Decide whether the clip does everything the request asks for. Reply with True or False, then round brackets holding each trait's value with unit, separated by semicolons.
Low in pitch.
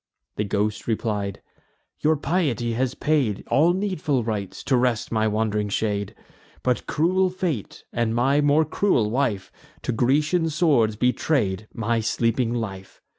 True (120 Hz)